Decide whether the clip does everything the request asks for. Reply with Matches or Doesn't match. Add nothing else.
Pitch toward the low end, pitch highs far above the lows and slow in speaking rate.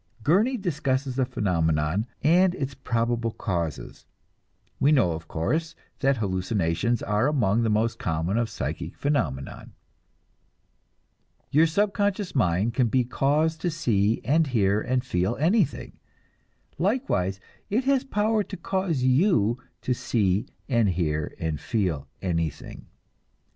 Matches